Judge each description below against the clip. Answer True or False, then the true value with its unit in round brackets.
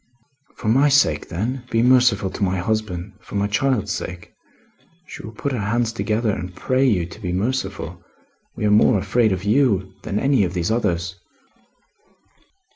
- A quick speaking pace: False (165 wpm)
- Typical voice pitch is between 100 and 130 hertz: True (105 Hz)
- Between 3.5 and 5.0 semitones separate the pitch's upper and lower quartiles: True (4.5 semitones)